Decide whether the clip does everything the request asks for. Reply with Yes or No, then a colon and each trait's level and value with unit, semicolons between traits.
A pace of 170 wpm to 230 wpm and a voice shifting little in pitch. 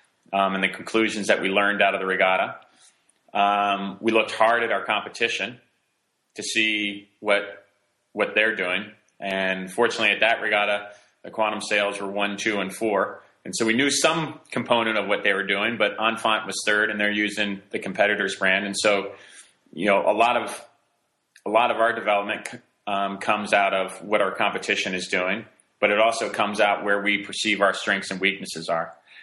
Yes: average, 190 wpm; narrow, 1.5 semitones